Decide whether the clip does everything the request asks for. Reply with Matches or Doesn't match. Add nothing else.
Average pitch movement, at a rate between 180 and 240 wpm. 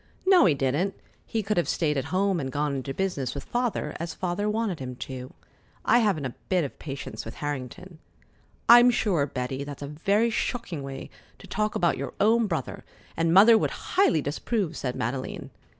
Doesn't match